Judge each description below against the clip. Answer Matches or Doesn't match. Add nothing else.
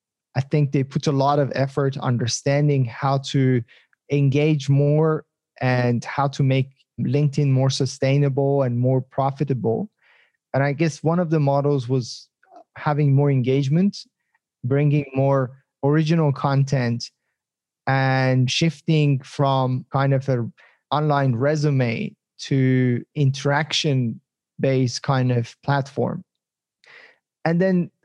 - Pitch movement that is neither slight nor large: Doesn't match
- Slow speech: Matches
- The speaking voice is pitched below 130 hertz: Doesn't match